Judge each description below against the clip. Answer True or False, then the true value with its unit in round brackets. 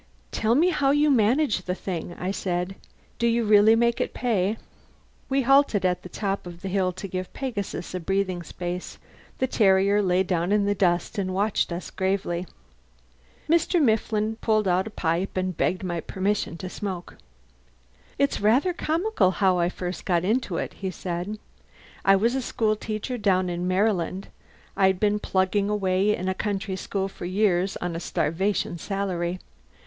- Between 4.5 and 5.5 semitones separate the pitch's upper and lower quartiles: False (3.0 semitones)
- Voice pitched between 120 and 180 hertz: False (195 Hz)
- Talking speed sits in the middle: True (170 wpm)